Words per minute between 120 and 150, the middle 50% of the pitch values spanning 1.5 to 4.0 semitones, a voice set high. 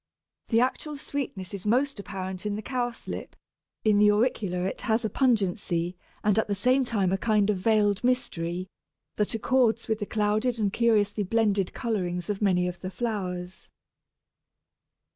No: average, 160 wpm; average, 3.4 semitones; high, 210 Hz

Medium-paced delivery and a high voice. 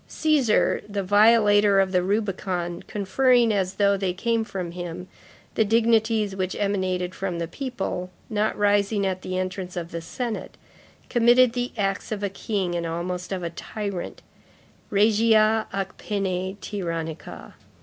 Yes: average, 145 wpm; high, 200 Hz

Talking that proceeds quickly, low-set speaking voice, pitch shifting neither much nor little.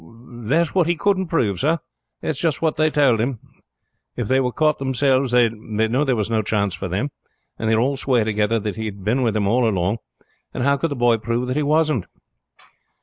Yes: fast, 220 wpm; low, 125 Hz; average, 4.7 semitones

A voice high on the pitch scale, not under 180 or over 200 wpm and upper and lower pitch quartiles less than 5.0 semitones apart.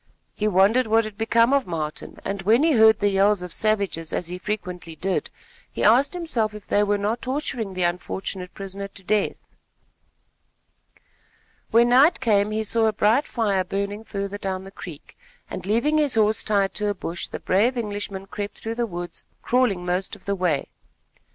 Yes: high, 205 Hz; average, 185 wpm; average, 2.8 semitones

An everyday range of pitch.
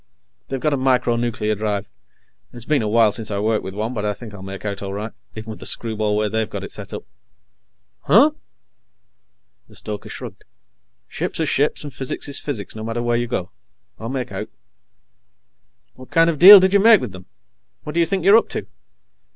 Yes: average, 4.9 semitones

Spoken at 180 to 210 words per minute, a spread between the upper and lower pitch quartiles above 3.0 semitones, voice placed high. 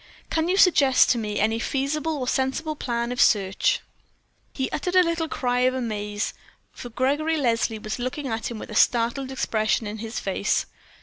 Yes: average, 185 wpm; average, 4.5 semitones; very high, 250 Hz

